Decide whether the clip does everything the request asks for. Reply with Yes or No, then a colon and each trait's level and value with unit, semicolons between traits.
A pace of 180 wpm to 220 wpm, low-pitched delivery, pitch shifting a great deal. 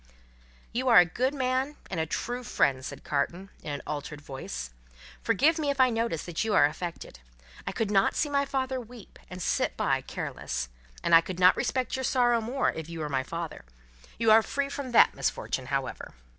No: average, 200 wpm; high, 220 Hz; wide, 7.9 semitones